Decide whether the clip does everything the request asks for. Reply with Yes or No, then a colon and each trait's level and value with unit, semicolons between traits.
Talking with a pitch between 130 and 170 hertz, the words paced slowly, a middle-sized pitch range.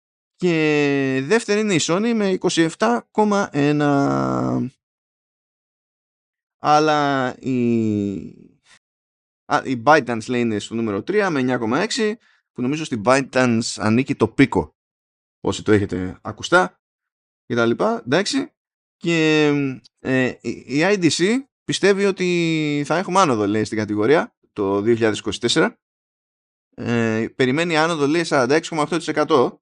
No: medium, 140 Hz; slow, 105 wpm; wide, 6.8 semitones